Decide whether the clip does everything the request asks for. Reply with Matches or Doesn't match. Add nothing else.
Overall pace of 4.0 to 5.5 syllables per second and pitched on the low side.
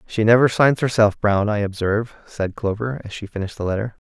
Doesn't match